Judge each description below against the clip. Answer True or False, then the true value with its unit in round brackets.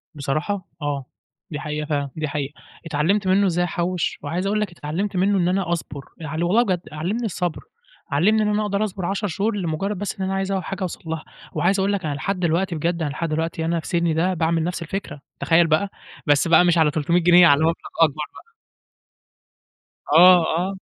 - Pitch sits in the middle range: True (175 Hz)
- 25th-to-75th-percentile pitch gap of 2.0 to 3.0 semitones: False (3.5 semitones)